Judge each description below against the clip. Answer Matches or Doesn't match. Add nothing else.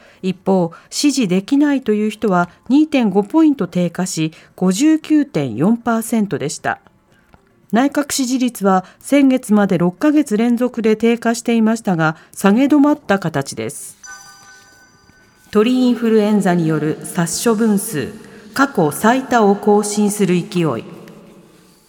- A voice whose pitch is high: Matches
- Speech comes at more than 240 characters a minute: Doesn't match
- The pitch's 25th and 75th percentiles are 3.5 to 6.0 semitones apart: Matches